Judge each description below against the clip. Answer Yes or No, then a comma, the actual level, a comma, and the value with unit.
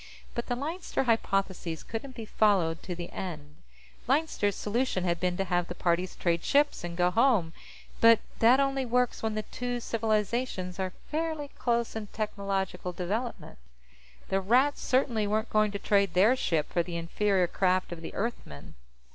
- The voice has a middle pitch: No, high, 205 Hz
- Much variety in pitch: No, average, 5.0 semitones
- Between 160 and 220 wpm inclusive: Yes, average, 165 wpm